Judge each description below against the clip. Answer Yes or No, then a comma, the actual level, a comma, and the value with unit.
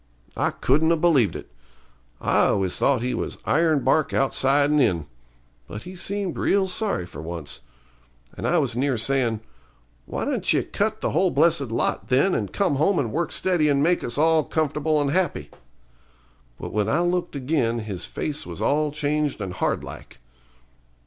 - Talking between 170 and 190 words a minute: Yes, average, 175 wpm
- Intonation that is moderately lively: No, wide, 5.7 semitones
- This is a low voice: No, medium, 145 Hz